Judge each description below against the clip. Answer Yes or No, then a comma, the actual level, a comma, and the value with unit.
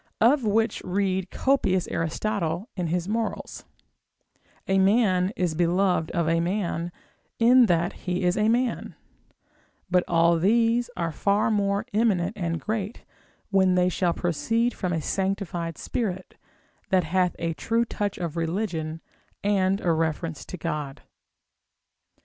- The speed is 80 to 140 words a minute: Yes, slow, 135 wpm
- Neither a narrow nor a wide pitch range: Yes, average, 3.9 semitones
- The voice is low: No, medium, 185 Hz